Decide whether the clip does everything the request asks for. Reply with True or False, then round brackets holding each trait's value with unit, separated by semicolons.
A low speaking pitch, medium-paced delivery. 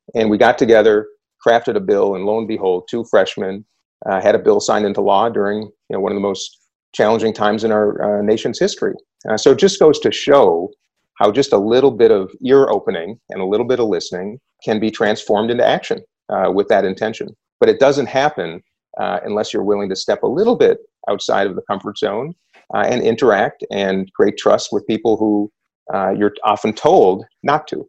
False (110 Hz; 210 wpm)